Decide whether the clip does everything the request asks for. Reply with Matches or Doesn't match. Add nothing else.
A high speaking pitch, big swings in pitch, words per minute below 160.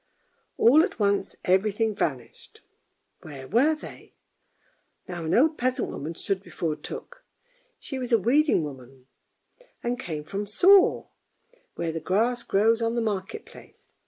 Matches